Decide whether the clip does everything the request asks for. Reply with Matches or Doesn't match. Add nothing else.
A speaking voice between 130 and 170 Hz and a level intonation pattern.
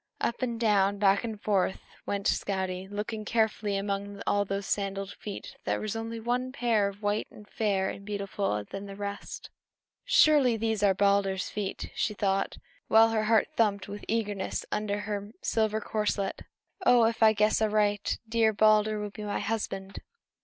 Doesn't match